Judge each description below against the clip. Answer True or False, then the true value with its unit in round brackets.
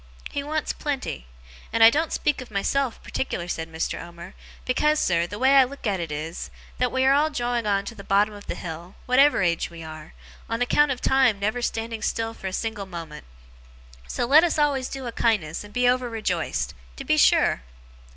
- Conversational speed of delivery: False (210 wpm)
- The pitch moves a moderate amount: False (6.8 semitones)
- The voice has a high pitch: True (225 Hz)